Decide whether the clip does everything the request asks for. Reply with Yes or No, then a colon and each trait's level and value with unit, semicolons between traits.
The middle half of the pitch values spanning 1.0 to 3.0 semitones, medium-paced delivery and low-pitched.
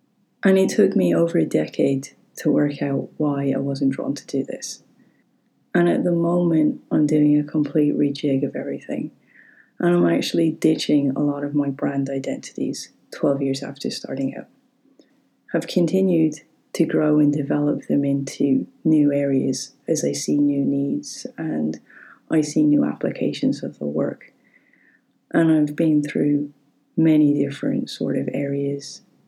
No: narrow, 2.4 semitones; average, 155 wpm; medium, 145 Hz